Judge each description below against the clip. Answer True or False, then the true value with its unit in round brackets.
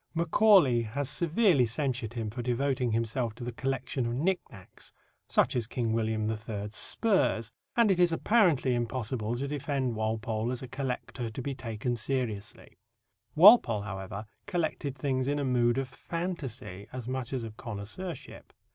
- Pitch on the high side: False (125 Hz)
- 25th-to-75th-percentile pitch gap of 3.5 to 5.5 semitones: True (3.9 semitones)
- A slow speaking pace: False (155 wpm)